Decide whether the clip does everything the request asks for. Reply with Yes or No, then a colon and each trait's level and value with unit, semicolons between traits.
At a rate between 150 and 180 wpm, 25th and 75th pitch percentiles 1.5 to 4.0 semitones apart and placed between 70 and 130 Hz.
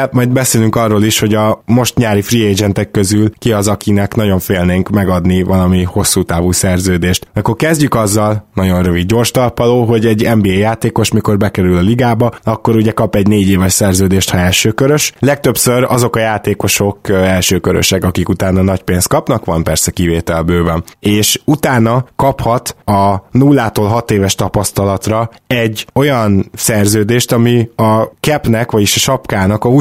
Yes: fast, 155 wpm; average, 3.7 semitones; low, 105 Hz